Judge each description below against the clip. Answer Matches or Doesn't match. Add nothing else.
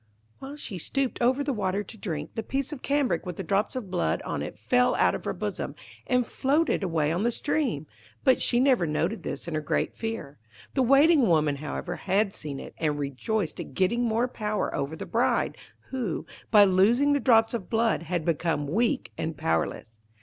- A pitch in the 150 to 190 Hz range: Doesn't match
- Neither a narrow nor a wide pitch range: Doesn't match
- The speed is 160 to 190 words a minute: Doesn't match